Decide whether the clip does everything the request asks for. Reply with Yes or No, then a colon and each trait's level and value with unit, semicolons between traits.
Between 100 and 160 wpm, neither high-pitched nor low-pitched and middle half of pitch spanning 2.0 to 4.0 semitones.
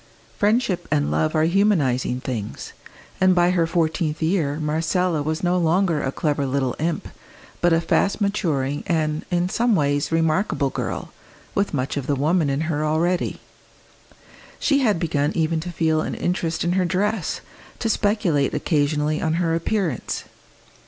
Yes: average, 155 wpm; medium, 160 Hz; average, 3.6 semitones